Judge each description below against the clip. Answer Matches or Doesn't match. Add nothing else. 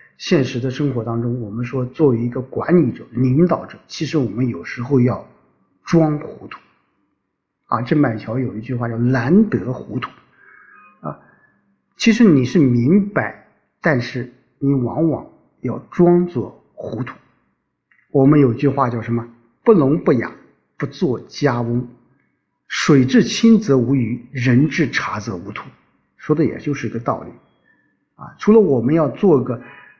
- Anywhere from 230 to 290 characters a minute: Doesn't match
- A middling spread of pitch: Matches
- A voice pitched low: Matches